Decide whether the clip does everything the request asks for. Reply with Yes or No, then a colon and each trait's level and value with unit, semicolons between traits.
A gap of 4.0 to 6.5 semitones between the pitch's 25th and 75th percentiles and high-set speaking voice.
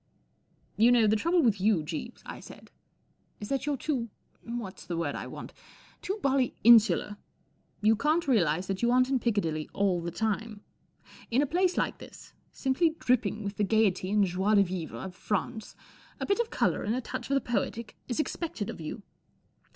Yes: average, 4.7 semitones; high, 220 Hz